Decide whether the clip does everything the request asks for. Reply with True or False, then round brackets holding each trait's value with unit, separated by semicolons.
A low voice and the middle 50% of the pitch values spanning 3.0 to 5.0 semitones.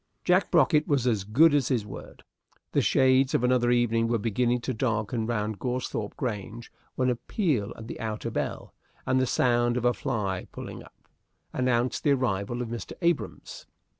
False (120 Hz; 2.6 semitones)